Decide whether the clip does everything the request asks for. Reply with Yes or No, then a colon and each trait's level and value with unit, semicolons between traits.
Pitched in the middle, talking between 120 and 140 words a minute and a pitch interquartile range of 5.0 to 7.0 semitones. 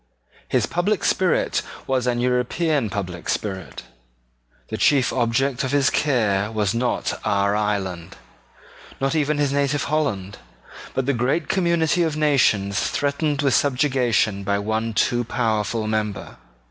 No: low, 125 Hz; slow, 135 wpm; average, 5.3 semitones